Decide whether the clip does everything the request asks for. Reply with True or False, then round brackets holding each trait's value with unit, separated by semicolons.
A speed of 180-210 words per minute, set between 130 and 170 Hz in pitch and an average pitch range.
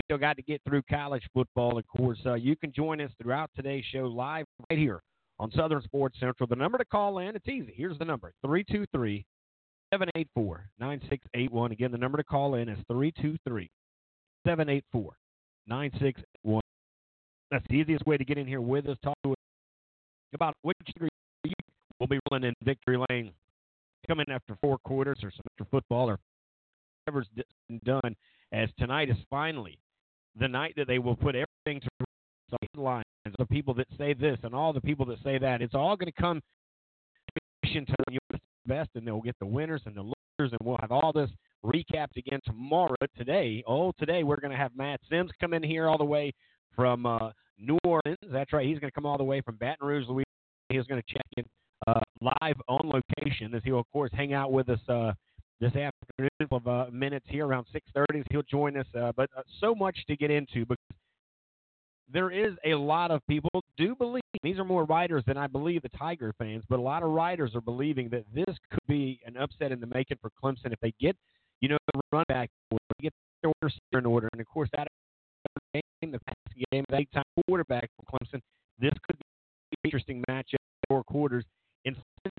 True (200 wpm; 135 Hz; 3.8 semitones)